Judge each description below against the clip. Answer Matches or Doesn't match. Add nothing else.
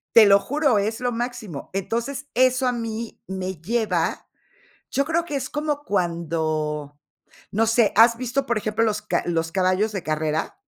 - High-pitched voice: Matches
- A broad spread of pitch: Matches